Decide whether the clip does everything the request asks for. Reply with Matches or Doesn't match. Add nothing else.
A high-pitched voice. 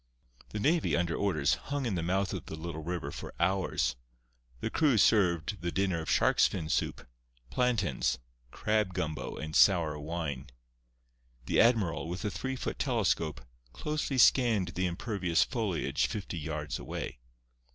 Doesn't match